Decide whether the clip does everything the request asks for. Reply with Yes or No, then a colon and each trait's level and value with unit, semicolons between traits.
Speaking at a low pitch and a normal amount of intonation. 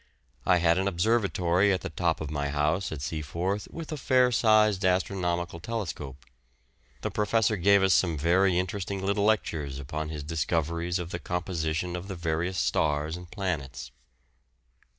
Yes: very low, 90 Hz; average, 3.7 semitones